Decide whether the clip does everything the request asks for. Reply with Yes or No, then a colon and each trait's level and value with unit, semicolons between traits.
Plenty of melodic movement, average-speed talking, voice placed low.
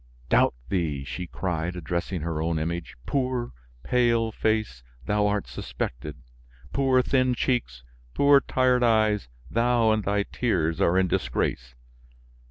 No: wide, 6.7 semitones; slow, 130 wpm; low, 105 Hz